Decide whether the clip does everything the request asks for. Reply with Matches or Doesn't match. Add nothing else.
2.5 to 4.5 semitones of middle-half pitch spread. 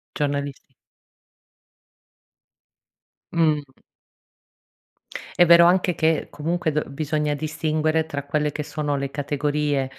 Doesn't match